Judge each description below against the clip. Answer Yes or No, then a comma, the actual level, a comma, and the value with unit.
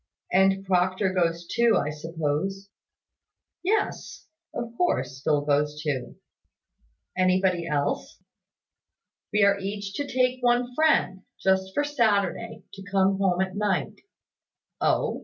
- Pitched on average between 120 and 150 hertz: No, high, 190 Hz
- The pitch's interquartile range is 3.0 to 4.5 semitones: Yes, average, 3.7 semitones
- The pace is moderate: No, slow, 120 wpm